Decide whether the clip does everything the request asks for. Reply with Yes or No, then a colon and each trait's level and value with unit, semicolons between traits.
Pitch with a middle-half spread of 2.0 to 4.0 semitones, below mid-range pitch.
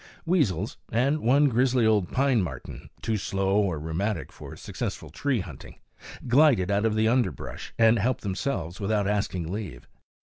No: average, 4.5 semitones; low, 110 Hz